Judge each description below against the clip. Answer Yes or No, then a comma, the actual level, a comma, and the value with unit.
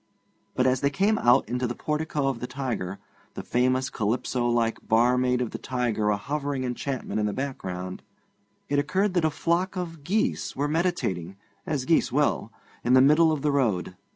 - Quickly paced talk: No, average, 180 wpm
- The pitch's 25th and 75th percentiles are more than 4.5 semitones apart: No, average, 4.1 semitones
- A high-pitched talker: No, low, 130 Hz